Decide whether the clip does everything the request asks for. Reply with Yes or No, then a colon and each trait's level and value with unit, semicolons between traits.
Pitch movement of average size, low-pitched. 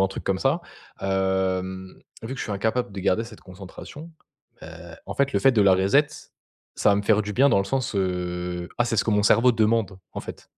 Yes: average, 3.6 semitones; low, 100 Hz